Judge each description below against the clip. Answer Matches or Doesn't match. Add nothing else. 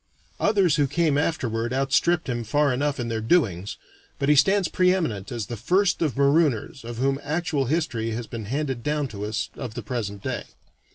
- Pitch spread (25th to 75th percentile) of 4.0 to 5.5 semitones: Matches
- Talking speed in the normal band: Matches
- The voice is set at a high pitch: Doesn't match